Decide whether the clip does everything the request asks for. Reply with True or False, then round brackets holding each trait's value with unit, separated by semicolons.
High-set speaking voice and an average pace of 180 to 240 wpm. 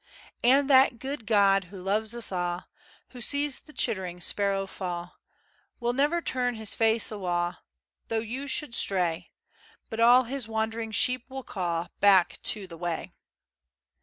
False (220 Hz; 150 wpm)